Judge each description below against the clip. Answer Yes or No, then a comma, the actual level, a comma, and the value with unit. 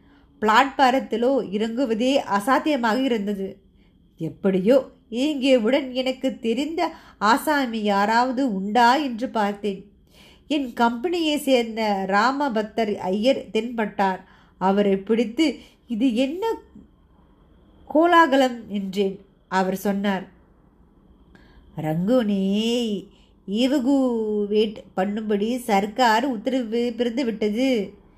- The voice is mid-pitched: No, high, 230 Hz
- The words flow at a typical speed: No, slow, 70 wpm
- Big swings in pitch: No, average, 4.5 semitones